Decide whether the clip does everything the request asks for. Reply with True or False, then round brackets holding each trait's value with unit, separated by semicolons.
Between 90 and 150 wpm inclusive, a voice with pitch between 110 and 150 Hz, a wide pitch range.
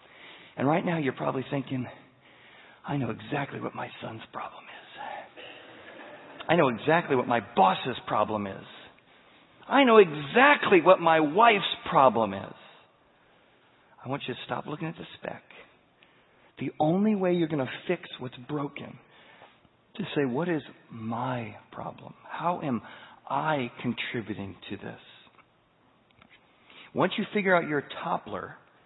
True (140 wpm; 140 Hz; 5.7 semitones)